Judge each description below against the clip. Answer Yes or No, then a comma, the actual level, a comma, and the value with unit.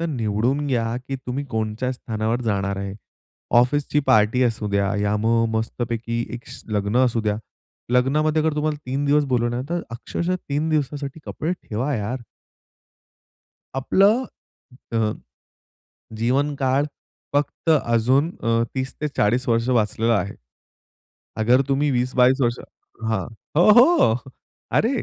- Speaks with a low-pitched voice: Yes, low, 125 Hz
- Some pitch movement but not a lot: Yes, average, 4.3 semitones